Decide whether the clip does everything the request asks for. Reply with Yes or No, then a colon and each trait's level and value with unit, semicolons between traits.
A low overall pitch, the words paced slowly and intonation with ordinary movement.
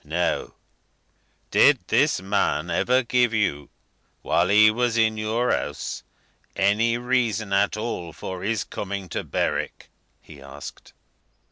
Yes: low, 105 Hz; slow, 125 wpm; average, 4.4 semitones